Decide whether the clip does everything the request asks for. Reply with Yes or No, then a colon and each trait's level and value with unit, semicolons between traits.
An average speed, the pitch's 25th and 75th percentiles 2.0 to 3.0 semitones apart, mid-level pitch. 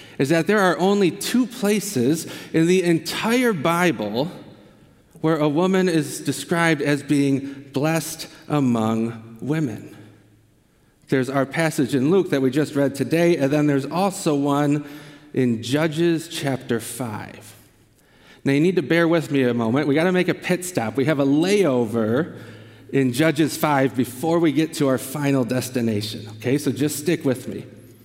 No: average, 165 wpm; average, 4.6 semitones; medium, 145 Hz